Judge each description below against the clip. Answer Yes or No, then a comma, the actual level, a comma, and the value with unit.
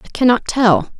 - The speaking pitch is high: Yes, high, 235 Hz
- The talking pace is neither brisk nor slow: Yes, average, 180 wpm